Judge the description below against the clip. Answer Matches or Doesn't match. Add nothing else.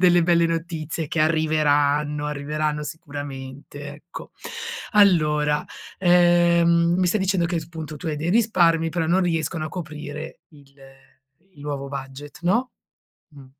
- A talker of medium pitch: Matches